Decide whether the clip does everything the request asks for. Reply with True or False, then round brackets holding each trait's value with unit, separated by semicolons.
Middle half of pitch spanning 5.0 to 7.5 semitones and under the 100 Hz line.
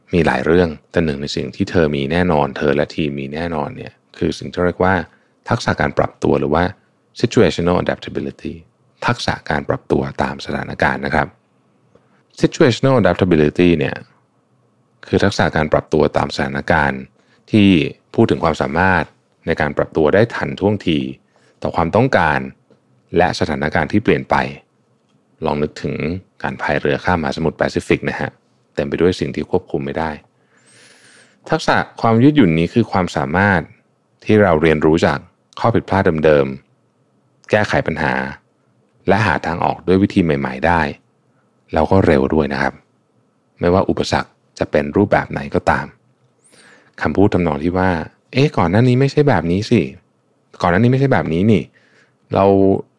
True (5.4 semitones; 85 Hz)